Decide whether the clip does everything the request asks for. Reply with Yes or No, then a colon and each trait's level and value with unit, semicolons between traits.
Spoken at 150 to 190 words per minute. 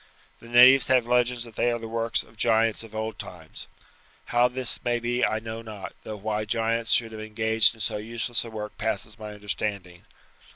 No: average, 200 wpm